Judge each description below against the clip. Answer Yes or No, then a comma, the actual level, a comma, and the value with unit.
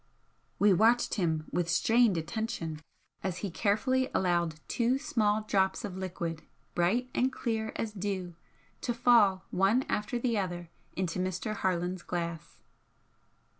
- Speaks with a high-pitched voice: Yes, high, 195 Hz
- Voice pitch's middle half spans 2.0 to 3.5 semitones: No, average, 4.5 semitones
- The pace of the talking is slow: Yes, slow, 130 wpm